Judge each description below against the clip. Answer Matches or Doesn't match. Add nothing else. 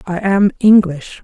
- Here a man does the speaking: Doesn't match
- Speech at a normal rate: Matches